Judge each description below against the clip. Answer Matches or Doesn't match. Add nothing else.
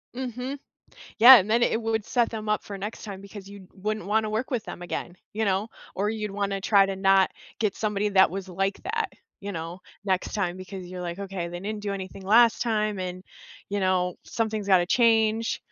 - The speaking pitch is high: Matches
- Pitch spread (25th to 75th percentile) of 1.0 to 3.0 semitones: Matches